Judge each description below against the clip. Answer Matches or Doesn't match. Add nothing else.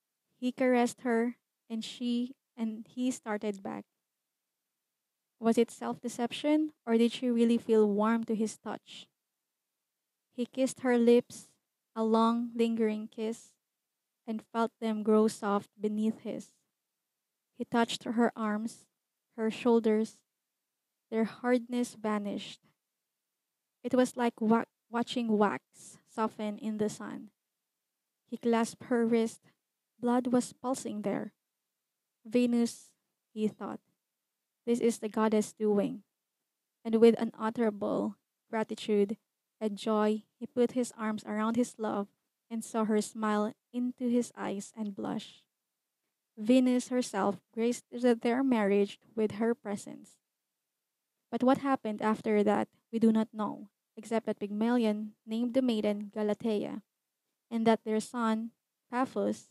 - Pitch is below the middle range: Doesn't match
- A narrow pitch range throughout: Matches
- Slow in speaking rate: Matches